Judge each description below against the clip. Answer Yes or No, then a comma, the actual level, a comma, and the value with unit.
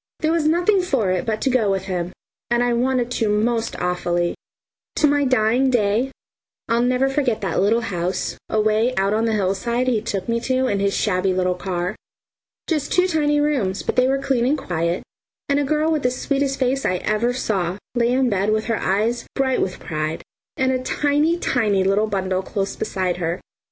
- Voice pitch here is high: Yes, high, 230 Hz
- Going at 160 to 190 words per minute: No, average, 200 wpm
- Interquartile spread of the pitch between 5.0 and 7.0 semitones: Yes, wide, 5.4 semitones